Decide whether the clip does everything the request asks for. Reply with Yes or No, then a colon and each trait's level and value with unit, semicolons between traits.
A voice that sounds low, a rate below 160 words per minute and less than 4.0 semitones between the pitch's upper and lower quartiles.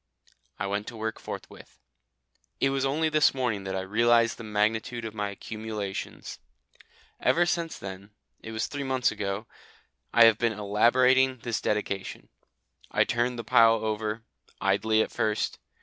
Yes: low, 110 Hz; average, 150 wpm; average, 2.8 semitones